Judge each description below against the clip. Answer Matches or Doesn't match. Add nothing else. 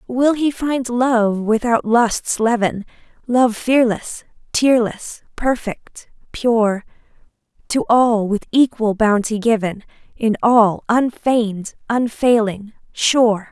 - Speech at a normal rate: Doesn't match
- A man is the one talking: Doesn't match